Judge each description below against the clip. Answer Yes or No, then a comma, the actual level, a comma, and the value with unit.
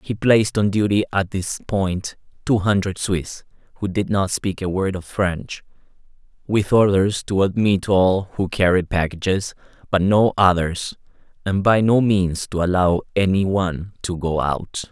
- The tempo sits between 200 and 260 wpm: No, average, 160 wpm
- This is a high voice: No, very low, 95 Hz